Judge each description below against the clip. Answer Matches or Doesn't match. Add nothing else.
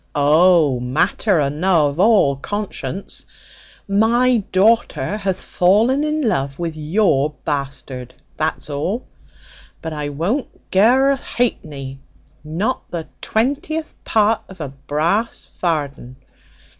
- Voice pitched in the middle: Matches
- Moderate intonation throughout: Doesn't match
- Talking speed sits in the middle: Doesn't match